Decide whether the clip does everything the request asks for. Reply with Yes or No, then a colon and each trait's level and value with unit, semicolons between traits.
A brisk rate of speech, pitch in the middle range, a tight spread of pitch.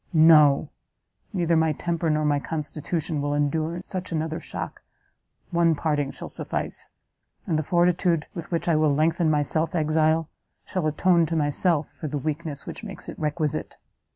No: average, 160 wpm; medium, 155 Hz; narrow, 1.9 semitones